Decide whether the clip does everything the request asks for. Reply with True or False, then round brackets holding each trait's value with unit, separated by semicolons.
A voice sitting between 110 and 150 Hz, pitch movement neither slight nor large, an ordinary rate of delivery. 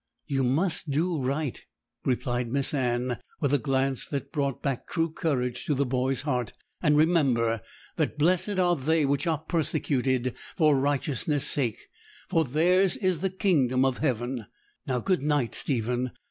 True (140 Hz; 3.9 semitones; 155 wpm)